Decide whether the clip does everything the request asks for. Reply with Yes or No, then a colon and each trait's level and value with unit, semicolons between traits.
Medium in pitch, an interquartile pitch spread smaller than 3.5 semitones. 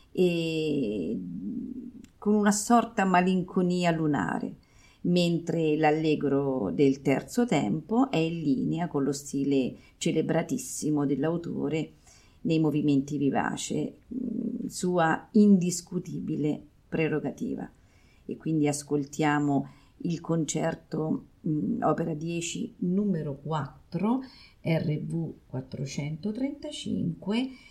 No: medium, 165 Hz; average, 5.0 semitones